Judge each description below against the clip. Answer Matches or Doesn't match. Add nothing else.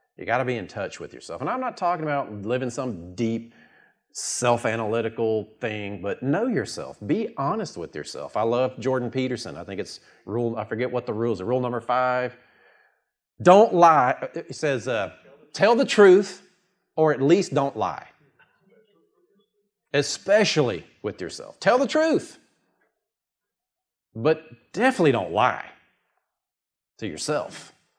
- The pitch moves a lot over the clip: Matches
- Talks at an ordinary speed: Matches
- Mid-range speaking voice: Doesn't match